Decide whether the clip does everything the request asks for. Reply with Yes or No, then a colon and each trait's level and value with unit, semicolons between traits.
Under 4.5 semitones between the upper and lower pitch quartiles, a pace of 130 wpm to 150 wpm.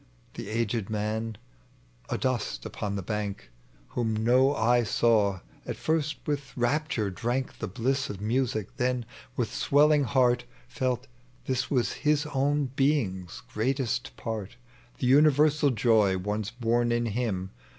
Yes: average, 3.9 semitones; average, 140 wpm